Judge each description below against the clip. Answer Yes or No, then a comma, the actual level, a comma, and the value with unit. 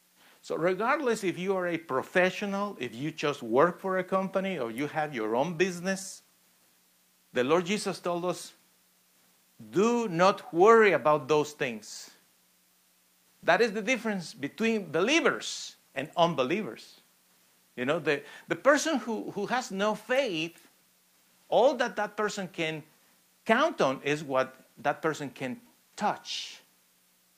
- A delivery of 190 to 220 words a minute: No, slow, 135 wpm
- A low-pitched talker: No, medium, 165 Hz